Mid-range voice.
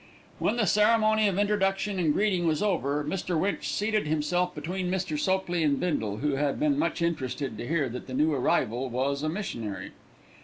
Yes: medium, 170 Hz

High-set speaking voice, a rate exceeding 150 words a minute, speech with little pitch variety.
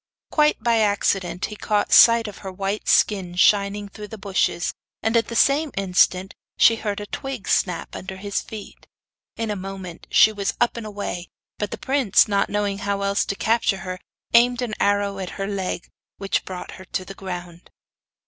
Yes: high, 200 Hz; average, 185 wpm; narrow, 2.3 semitones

